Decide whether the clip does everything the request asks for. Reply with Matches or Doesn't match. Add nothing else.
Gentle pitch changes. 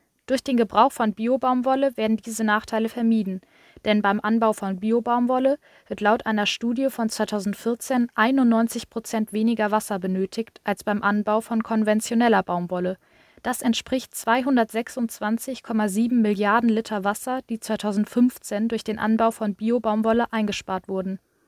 Matches